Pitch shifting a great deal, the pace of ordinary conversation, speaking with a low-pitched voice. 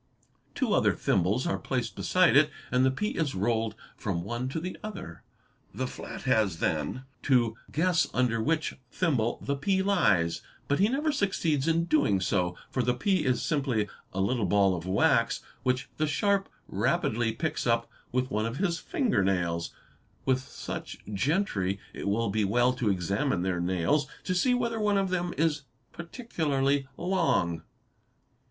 Yes: wide, 8.6 semitones; average, 160 wpm; low, 130 Hz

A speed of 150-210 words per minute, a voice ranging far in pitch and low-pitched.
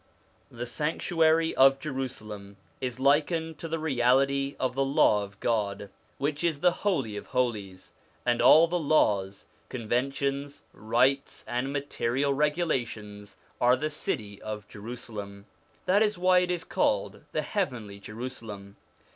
No: slow, 135 wpm; wide, 5.9 semitones; low, 130 Hz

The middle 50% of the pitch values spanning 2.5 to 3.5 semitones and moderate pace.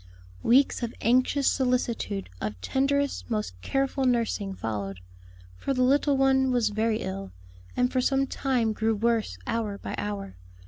No: average, 4.8 semitones; average, 145 wpm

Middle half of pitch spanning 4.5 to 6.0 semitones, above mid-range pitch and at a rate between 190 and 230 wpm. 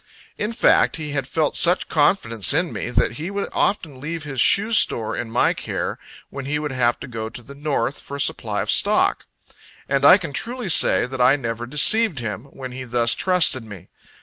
No: average, 5.1 semitones; medium, 140 Hz; fast, 205 wpm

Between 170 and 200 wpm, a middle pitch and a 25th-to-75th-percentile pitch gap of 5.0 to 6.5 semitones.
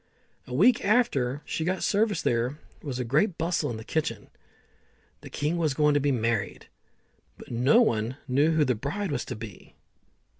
Yes: average, 175 wpm; medium, 145 Hz; wide, 5.5 semitones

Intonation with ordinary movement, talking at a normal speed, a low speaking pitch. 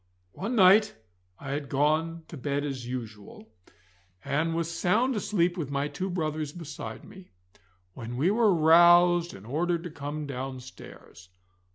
No: average, 4.1 semitones; average, 145 wpm; medium, 160 Hz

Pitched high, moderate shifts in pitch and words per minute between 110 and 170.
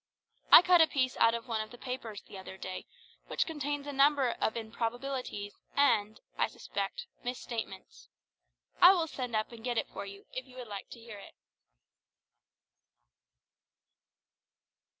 Yes: high, 240 Hz; average, 4.1 semitones; average, 155 wpm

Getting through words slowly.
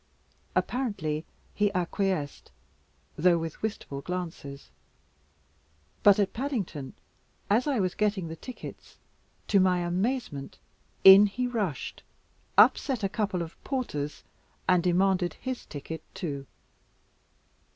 Yes: slow, 110 wpm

